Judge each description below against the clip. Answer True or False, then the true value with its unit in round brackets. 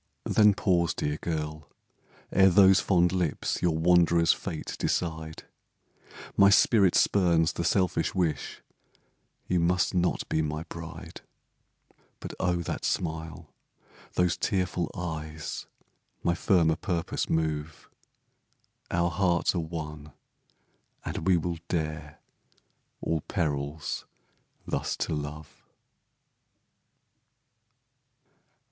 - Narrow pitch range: True (2.3 semitones)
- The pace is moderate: False (100 wpm)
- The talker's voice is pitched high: False (85 Hz)